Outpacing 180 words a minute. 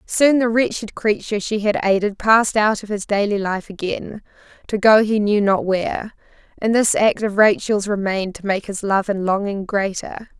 Yes: average, 190 wpm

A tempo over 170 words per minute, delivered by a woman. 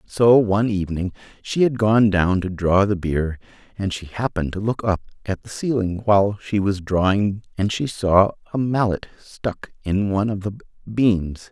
No: average, 180 wpm; male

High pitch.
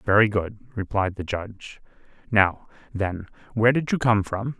No: low, 105 Hz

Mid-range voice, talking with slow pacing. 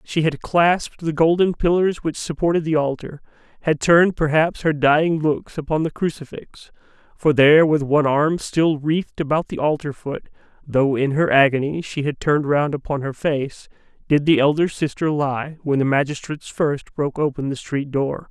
No: medium, 150 Hz; average, 175 wpm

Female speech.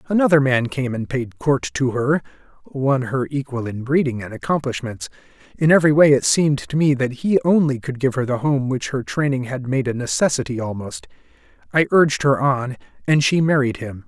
No: male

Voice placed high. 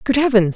Yes: high, 235 Hz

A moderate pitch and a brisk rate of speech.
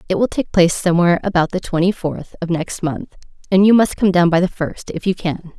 Yes: medium, 180 Hz; fast, 245 wpm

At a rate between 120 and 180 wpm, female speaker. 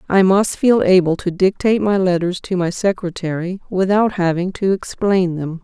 Yes: average, 170 wpm; female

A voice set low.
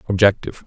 Yes: low, 100 Hz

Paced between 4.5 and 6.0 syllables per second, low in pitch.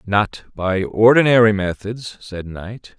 No: 3.7 syllables/s; low, 105 Hz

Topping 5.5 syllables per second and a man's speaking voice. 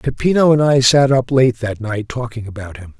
No: 5.1 syllables/s; male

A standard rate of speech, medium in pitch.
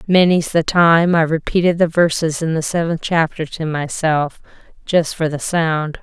Yes: average, 170 wpm; medium, 160 Hz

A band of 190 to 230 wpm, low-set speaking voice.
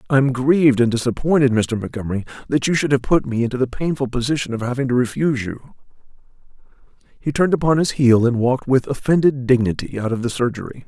Yes: average, 200 wpm; low, 130 Hz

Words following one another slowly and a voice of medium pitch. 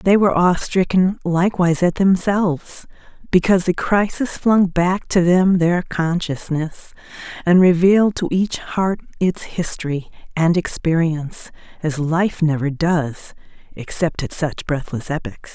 Yes: slow, 130 wpm; medium, 170 Hz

